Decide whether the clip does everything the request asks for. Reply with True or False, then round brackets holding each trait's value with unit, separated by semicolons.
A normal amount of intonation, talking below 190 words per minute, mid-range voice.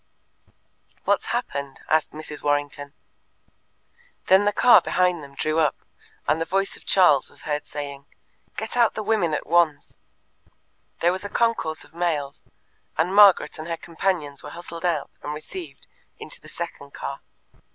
True (4.2 semitones; 155 wpm; 165 Hz)